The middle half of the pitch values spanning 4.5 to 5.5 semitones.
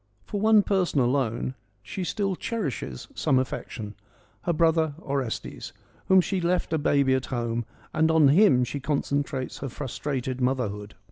Yes: average, 5.1 semitones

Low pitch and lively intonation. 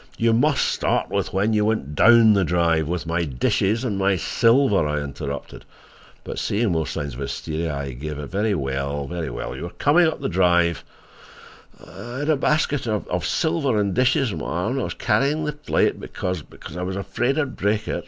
Yes: very low, 95 Hz; wide, 7.3 semitones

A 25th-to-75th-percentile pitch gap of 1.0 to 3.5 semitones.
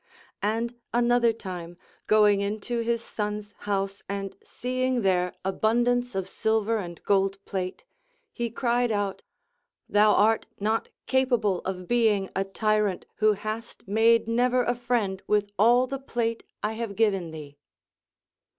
Yes: average, 3.1 semitones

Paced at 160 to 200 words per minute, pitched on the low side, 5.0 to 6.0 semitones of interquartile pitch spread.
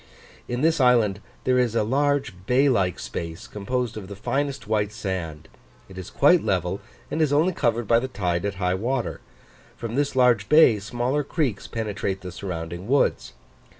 Yes: average, 175 wpm; low, 115 Hz; average, 5.3 semitones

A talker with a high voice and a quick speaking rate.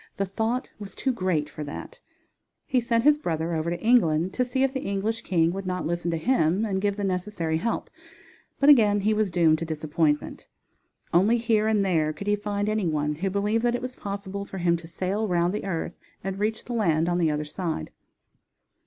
Yes: high, 195 Hz; fast, 215 wpm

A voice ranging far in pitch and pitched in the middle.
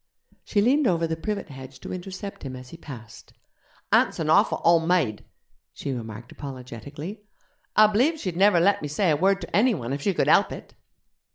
Yes: wide, 6.8 semitones; medium, 165 Hz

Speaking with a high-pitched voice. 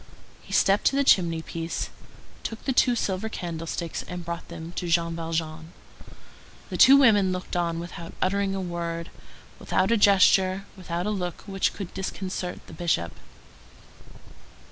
No: medium, 180 Hz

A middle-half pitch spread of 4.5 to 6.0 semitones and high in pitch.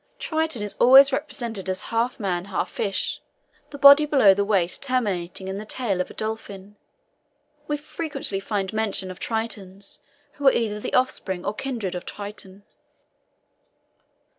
Yes: average, 4.9 semitones; high, 210 Hz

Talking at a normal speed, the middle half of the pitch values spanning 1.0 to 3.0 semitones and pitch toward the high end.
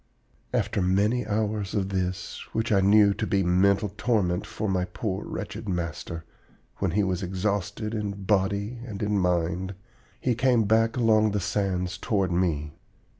No: average, 155 wpm; average, 2.7 semitones; low, 100 Hz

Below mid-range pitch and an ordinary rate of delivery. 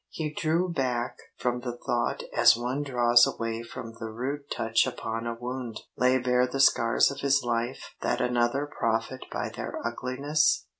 Yes: low, 125 Hz; average, 165 wpm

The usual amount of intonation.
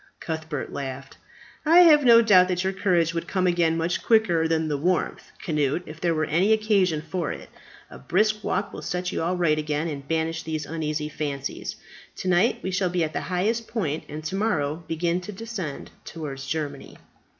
Yes: average, 3.5 semitones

